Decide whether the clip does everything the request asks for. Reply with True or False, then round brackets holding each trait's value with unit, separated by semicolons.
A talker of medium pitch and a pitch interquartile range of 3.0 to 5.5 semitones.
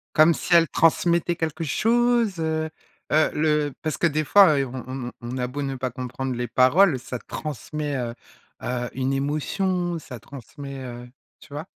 True (145 Hz; 4.2 semitones)